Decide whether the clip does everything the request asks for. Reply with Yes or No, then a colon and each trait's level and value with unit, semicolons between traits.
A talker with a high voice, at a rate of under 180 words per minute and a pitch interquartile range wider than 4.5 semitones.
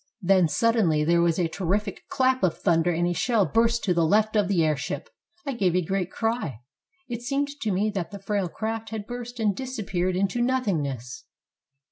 No: high, 200 Hz; average, 190 wpm; average, 5.0 semitones